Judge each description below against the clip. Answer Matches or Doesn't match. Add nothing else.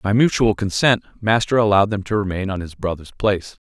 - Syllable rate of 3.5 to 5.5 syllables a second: Doesn't match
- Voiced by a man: Matches